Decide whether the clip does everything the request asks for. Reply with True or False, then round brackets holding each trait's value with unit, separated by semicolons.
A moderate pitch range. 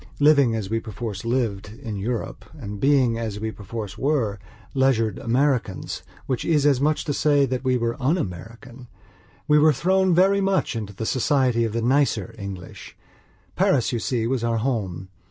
True (4.3 semitones)